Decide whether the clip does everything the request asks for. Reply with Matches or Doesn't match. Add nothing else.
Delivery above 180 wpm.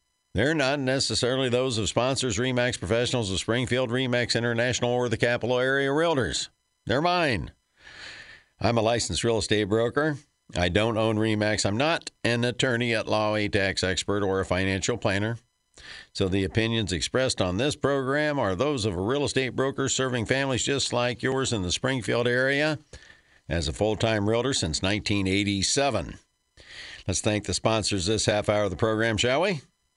Doesn't match